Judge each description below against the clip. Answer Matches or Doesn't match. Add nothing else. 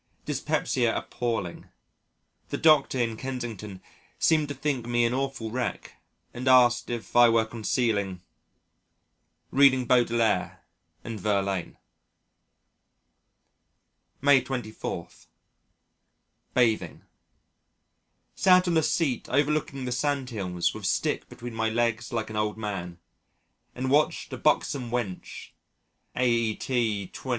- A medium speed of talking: Doesn't match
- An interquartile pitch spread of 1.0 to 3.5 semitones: Matches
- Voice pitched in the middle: Doesn't match